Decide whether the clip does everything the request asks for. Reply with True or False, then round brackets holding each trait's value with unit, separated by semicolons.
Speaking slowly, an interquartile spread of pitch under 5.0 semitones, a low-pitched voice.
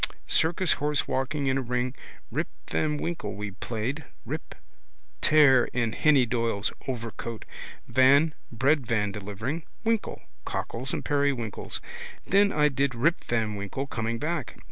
True (130 wpm; 4.4 semitones; 130 Hz)